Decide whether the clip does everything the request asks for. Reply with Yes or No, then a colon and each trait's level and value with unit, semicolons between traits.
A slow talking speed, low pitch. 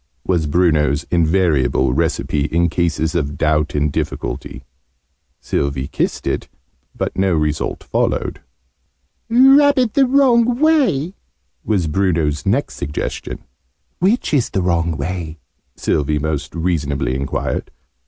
Yes: slow, 115 wpm; very low, 85 Hz